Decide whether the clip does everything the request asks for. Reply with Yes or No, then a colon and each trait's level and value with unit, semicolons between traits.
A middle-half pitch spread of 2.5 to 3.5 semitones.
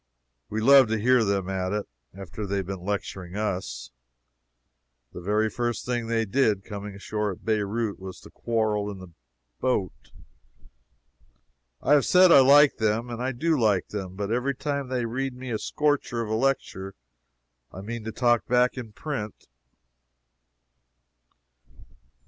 No: average, 3.9 semitones